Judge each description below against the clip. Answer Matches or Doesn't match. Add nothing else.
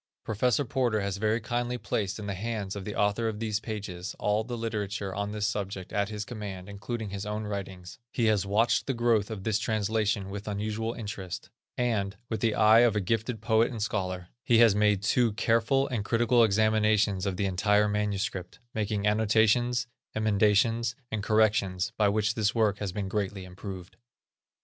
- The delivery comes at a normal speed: Matches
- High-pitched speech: Doesn't match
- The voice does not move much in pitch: Matches